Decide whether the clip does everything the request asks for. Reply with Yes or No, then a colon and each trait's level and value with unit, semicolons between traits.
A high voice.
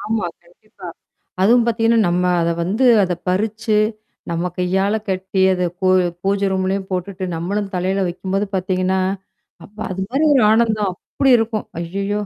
Yes: high, 195 Hz